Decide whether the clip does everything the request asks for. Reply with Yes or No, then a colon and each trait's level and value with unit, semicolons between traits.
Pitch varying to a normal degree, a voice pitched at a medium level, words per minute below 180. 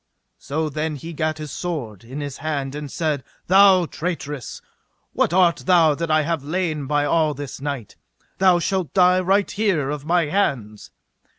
Yes: average, 3.6 semitones; medium, 155 Hz; average, 170 wpm